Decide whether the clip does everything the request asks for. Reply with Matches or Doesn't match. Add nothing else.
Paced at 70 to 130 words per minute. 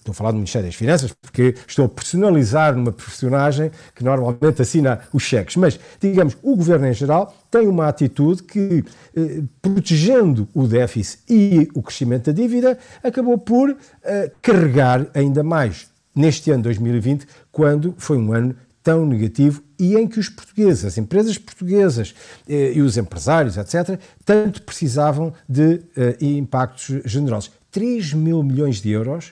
Doesn't match